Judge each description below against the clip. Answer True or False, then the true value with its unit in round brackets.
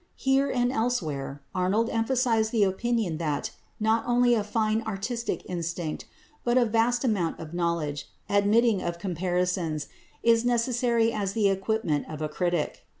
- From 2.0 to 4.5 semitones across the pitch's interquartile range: False (5.2 semitones)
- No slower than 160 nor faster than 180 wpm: False (145 wpm)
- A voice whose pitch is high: True (210 Hz)